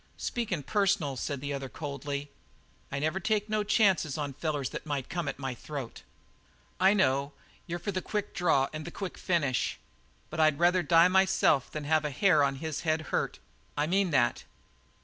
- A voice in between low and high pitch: Yes, medium, 155 Hz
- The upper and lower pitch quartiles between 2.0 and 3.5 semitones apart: No, average, 4.8 semitones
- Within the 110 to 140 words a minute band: No, average, 185 wpm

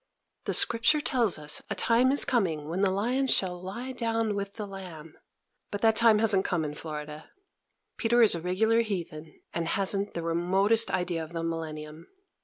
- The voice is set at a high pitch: Yes, high, 195 Hz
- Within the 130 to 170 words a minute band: No, average, 180 wpm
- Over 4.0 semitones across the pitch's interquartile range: Yes, wide, 5.5 semitones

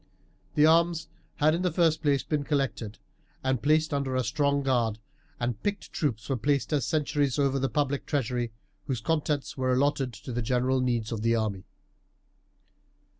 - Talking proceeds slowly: No, average, 170 wpm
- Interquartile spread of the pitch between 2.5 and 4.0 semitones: Yes, average, 3.4 semitones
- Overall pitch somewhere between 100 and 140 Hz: Yes, low, 135 Hz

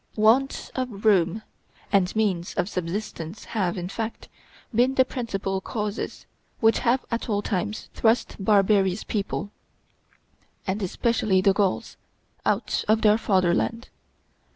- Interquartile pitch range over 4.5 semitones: No, average, 2.8 semitones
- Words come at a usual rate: No, slow, 125 wpm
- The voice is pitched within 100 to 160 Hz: No, high, 210 Hz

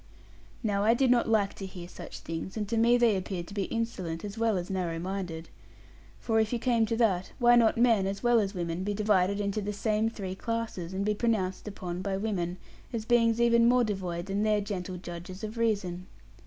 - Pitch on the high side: Yes, high, 205 Hz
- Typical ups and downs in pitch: Yes, average, 3.6 semitones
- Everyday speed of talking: No, fast, 220 wpm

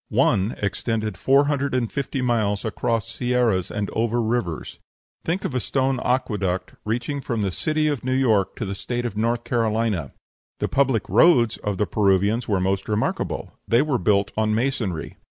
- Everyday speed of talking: Yes, average, 170 wpm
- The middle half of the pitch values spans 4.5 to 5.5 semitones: No, average, 3.8 semitones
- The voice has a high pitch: No, low, 115 Hz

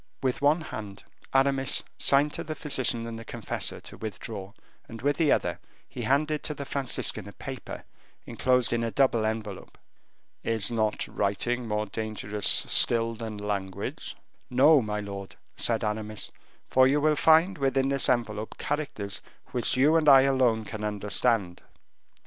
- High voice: No, low, 115 Hz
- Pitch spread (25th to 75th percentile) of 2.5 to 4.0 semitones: No, average, 4.4 semitones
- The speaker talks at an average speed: Yes, average, 155 wpm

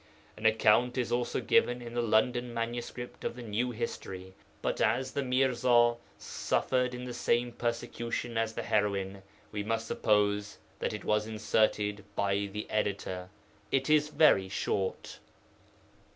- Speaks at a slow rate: No, average, 145 wpm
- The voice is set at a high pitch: No, low, 115 Hz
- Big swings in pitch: No, average, 2.8 semitones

